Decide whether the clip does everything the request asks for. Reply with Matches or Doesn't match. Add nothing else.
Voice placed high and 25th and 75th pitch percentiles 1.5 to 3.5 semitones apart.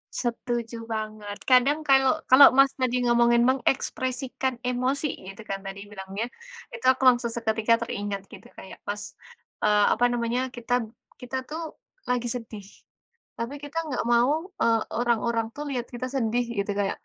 Matches